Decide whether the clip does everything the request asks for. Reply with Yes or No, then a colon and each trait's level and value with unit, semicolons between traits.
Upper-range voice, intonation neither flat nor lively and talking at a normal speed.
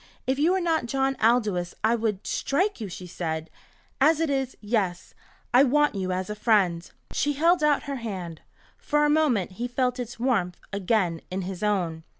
No: high, 230 Hz; wide, 6.9 semitones; average, 185 wpm